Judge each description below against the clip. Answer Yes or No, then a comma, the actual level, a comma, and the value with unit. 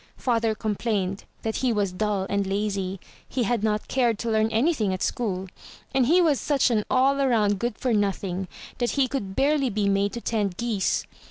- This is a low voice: No, high, 220 Hz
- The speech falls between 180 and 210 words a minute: Yes, average, 190 wpm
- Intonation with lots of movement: No, average, 3.7 semitones